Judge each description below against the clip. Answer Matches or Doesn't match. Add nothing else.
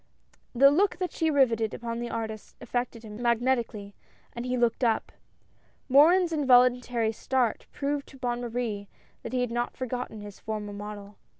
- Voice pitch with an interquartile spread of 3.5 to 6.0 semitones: Doesn't match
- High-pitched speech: Matches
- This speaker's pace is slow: Doesn't match